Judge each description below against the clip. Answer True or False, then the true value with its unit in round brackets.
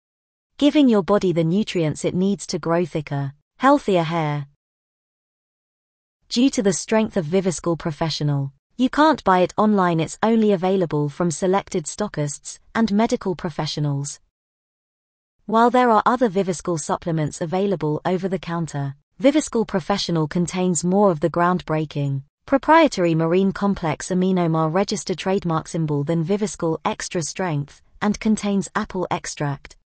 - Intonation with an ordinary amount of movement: True (4.2 semitones)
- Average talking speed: False (130 wpm)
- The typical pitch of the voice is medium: True (180 Hz)